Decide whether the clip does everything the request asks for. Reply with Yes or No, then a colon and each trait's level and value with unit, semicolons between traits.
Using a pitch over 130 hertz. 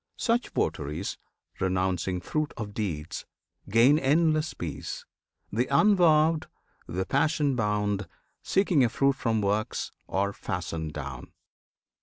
No: low, 110 Hz